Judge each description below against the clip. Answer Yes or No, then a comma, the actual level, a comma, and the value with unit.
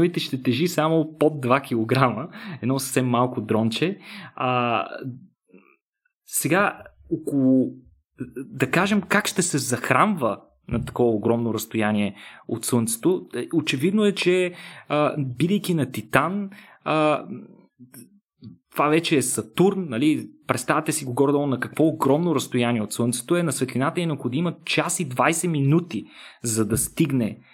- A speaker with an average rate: Yes, average, 130 wpm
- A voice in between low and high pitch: Yes, medium, 145 Hz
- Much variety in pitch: Yes, wide, 6.0 semitones